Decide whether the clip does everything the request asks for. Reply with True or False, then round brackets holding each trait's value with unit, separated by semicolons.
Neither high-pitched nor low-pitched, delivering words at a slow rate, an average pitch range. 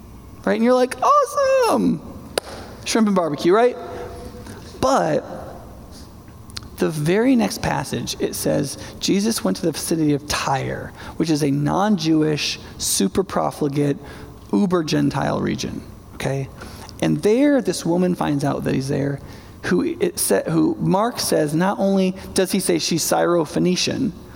False (160 Hz; 130 wpm; 5.8 semitones)